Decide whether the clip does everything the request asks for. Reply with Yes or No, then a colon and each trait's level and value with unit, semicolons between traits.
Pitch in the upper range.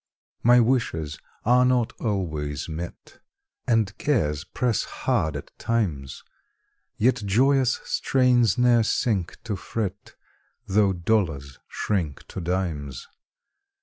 No: low, 100 Hz